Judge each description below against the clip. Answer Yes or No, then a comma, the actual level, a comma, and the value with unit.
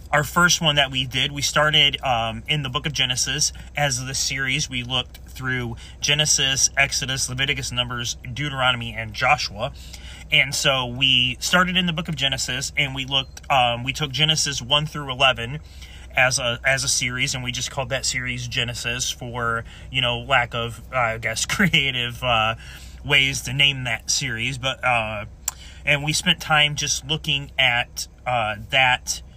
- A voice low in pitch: Yes, low, 130 Hz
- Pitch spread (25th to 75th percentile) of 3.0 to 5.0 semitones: Yes, average, 3.3 semitones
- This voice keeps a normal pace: Yes, average, 170 wpm